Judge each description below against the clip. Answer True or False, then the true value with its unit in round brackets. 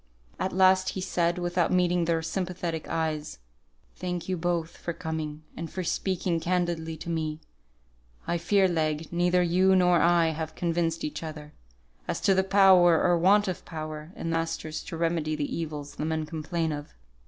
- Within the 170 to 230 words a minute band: True (175 wpm)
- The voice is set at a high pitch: False (170 Hz)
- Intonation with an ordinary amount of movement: False (2.0 semitones)